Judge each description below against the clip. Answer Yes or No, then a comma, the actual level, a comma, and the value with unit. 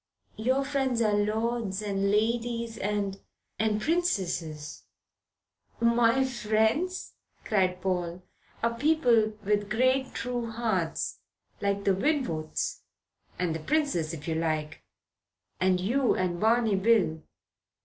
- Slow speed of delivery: Yes, slow, 115 wpm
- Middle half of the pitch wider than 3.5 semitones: Yes, average, 4.5 semitones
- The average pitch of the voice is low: No, high, 215 Hz